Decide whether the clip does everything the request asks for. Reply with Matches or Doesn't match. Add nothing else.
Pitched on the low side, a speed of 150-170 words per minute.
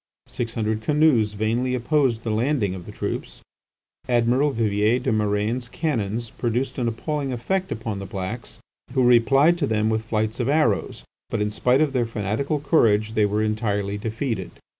Matches